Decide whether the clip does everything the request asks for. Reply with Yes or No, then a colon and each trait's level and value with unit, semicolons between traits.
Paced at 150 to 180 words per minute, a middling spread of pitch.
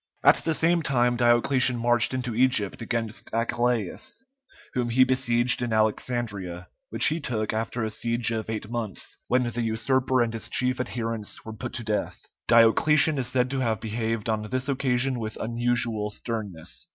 No: average, 165 wpm; narrow, 2.2 semitones